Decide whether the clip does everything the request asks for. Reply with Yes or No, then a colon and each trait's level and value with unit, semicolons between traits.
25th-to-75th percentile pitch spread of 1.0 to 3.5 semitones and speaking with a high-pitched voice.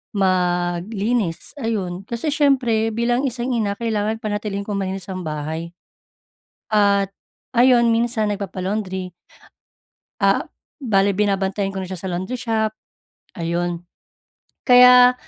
No: average, 3.9 semitones; high, 200 Hz